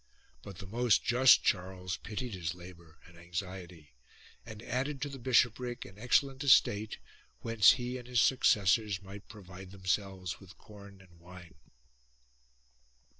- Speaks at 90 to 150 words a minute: Yes, average, 140 wpm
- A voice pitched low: Yes, low, 100 Hz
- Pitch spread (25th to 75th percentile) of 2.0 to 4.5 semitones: No, average, 4.9 semitones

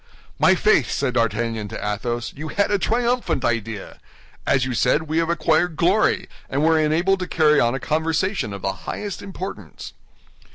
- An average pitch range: No, wide, 7.1 semitones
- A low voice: No, medium, 155 Hz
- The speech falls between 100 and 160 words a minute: No, average, 170 wpm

